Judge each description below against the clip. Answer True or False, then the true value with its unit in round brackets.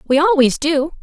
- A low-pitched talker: False (305 Hz)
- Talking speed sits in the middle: True (175 wpm)